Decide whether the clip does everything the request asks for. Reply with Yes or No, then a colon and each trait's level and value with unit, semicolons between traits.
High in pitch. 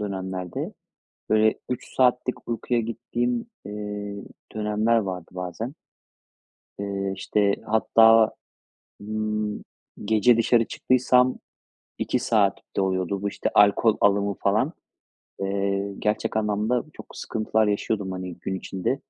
No: low, 105 Hz